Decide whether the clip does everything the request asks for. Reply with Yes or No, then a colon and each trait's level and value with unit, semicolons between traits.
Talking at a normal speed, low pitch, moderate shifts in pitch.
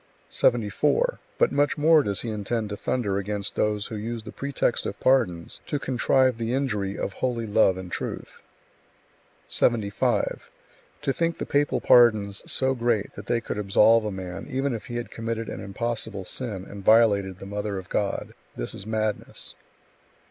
Yes: average, 170 wpm; low, 110 Hz; average, 3.5 semitones